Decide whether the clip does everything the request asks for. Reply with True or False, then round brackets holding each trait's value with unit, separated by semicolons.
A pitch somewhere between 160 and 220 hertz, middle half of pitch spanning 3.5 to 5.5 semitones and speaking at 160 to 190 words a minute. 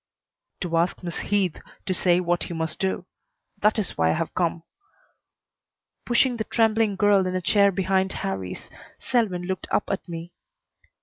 False (185 Hz; 3.0 semitones; 165 wpm)